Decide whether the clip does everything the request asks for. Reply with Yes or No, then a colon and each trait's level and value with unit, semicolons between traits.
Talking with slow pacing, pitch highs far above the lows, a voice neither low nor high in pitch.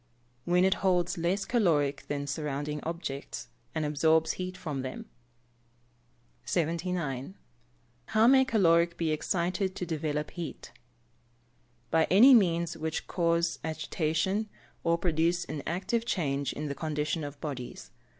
No: slow, 130 wpm; average, 3.3 semitones; medium, 165 Hz